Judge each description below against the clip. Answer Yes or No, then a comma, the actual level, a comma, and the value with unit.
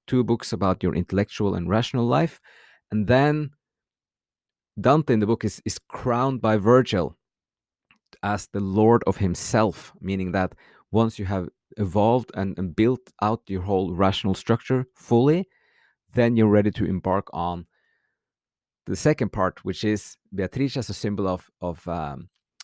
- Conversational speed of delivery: Yes, average, 150 wpm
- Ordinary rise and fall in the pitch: Yes, average, 4.0 semitones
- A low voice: Yes, low, 105 Hz